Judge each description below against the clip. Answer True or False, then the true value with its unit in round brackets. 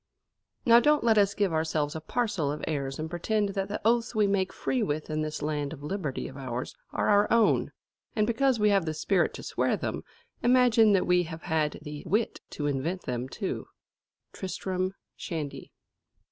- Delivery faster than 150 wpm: True (190 wpm)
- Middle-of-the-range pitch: True (180 Hz)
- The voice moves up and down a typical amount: False (5.7 semitones)